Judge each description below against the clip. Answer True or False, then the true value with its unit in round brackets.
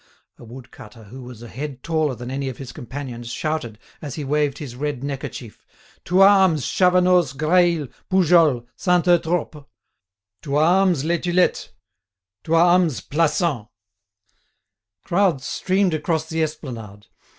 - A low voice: False (150 Hz)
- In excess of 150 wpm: False (135 wpm)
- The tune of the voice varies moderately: True (5.0 semitones)